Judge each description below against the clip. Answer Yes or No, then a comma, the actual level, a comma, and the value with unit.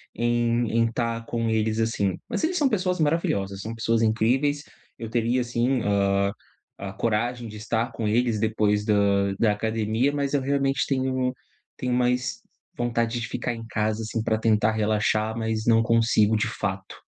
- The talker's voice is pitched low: Yes, low, 115 Hz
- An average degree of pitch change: No, narrow, 2.2 semitones